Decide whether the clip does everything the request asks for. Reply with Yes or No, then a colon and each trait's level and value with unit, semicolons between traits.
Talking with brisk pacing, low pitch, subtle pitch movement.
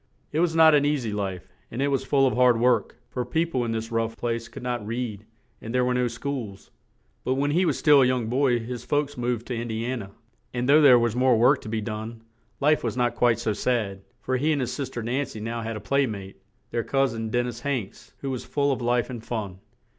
No: fast, 260 wpm; low, 120 Hz; average, 3.1 semitones